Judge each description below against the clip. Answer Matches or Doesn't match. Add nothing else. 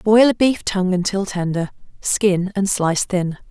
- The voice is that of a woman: Matches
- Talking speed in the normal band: Matches